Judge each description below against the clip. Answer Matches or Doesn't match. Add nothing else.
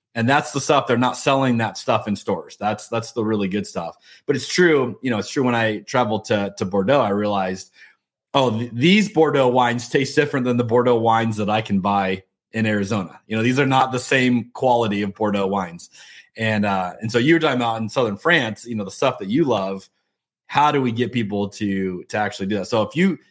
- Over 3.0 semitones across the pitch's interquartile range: Matches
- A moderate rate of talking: Doesn't match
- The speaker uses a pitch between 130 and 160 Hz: Doesn't match